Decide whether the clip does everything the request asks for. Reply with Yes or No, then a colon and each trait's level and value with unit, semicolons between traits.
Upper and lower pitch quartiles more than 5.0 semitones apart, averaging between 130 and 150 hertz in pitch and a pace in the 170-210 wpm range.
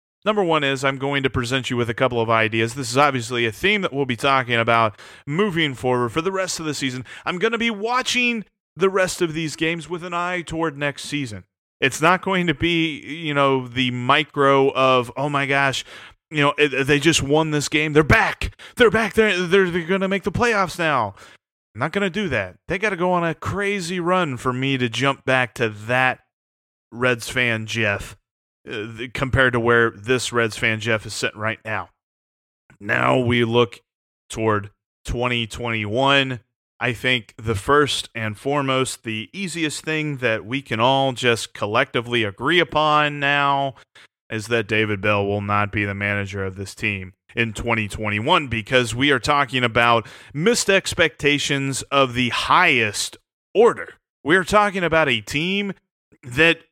Yes: wide, 5.6 semitones; low, 135 Hz; average, 180 wpm